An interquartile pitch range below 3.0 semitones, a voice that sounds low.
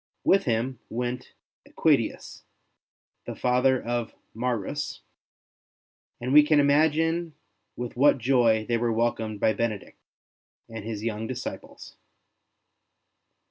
No: average, 3.6 semitones; low, 120 Hz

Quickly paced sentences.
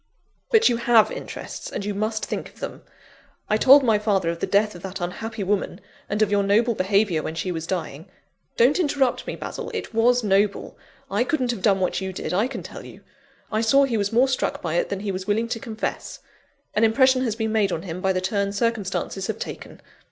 Yes: fast, 225 wpm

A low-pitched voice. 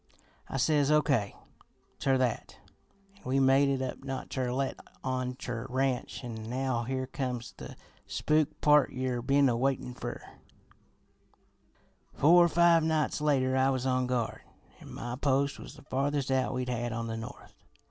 Yes: low, 130 Hz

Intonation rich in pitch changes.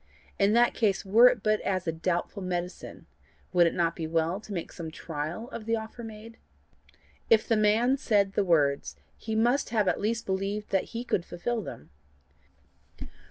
No: average, 4.4 semitones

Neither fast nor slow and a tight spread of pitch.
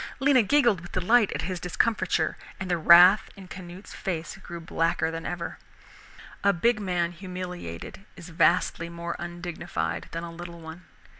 Yes: average, 155 wpm; narrow, 2.1 semitones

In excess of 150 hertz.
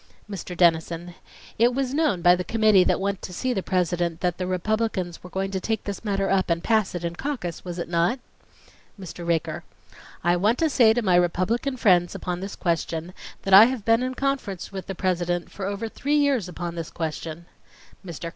Yes: medium, 185 Hz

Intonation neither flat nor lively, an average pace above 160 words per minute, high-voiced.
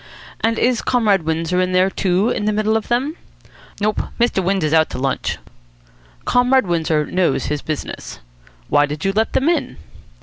No: wide, 5.7 semitones; average, 170 wpm; high, 195 Hz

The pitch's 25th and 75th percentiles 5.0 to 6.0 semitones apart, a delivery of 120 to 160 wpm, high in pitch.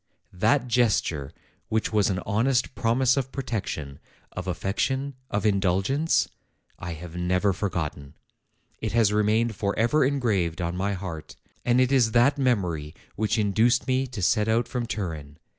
No: average, 5.3 semitones; average, 145 wpm; low, 105 Hz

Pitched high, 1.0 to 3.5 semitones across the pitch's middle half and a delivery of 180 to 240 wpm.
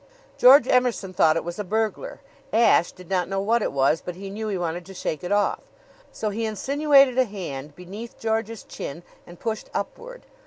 No: high, 205 Hz; average, 4.5 semitones; average, 195 wpm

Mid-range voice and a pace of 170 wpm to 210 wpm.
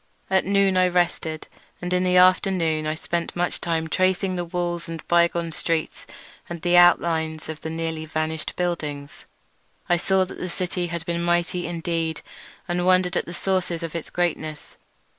Yes: medium, 170 Hz; average, 175 wpm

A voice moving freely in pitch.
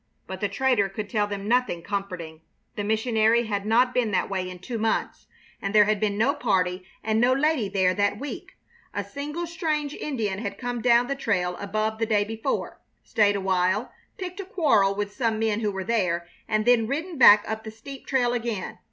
No: average, 3.7 semitones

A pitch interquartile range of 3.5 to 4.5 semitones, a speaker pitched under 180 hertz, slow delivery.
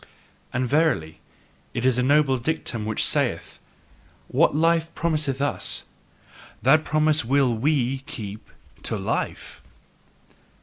Yes: average, 4.2 semitones; low, 135 Hz; slow, 115 wpm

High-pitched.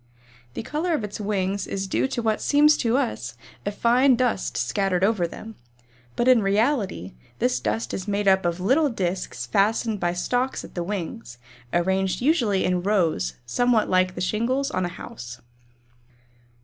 Yes: high, 200 Hz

